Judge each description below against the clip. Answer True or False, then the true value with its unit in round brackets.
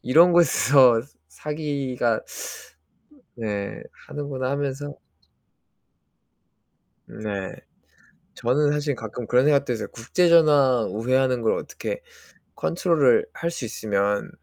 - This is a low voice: True (130 Hz)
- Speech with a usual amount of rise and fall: True (4.4 semitones)